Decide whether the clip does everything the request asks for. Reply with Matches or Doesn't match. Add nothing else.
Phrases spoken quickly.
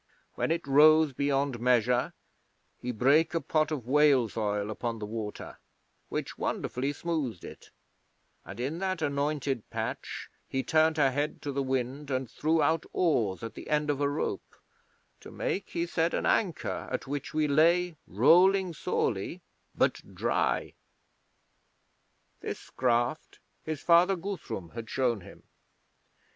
Doesn't match